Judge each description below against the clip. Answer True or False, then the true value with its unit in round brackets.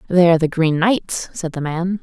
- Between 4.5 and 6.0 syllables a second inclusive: True (5.0 syllables/s)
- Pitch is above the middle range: False (175 Hz)